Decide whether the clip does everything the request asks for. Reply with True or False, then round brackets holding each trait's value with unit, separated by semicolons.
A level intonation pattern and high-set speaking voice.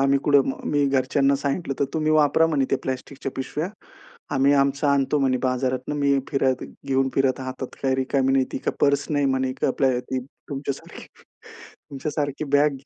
False (1.3 semitones; 135 Hz)